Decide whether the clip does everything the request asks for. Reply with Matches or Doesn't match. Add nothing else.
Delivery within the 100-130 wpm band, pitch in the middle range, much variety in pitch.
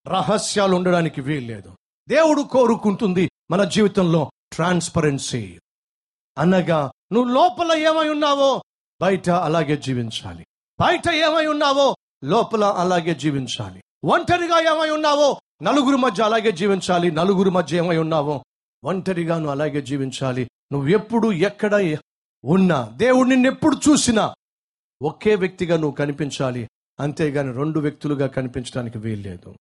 Matches